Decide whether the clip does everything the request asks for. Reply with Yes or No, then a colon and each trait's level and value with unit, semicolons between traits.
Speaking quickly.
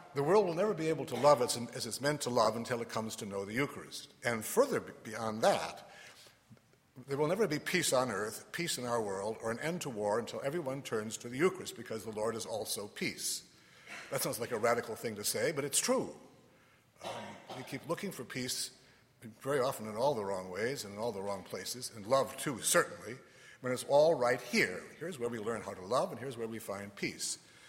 Yes: fast, 230 wpm